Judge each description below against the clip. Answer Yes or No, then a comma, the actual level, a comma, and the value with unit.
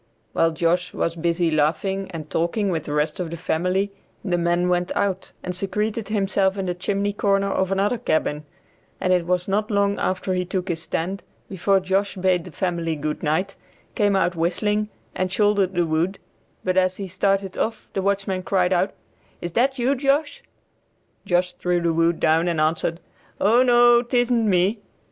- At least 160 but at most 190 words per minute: Yes, average, 180 wpm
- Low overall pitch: No, medium, 185 Hz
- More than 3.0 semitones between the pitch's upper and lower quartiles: No, average, 2.7 semitones